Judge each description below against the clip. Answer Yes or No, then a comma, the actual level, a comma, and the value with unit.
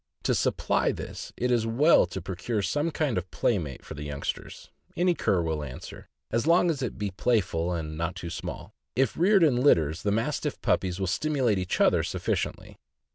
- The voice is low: Yes, low, 100 Hz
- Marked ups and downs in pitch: Yes, wide, 7.7 semitones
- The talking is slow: No, average, 185 wpm